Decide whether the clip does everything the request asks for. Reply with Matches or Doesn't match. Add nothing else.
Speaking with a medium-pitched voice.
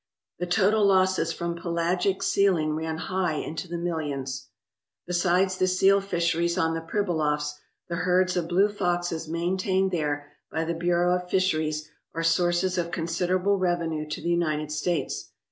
Matches